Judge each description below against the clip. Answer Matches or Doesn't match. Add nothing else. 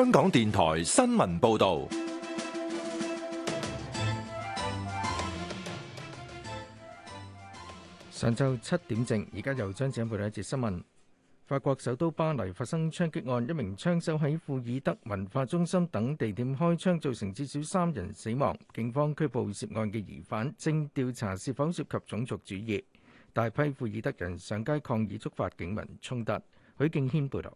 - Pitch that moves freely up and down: Matches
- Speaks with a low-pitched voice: Matches